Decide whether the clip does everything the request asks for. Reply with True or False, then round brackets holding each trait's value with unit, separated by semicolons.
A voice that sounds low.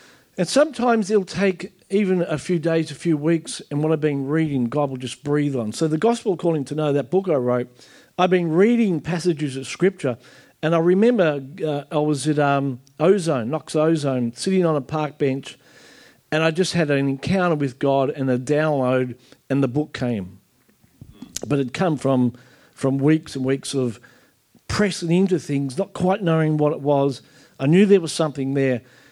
False (150 Hz)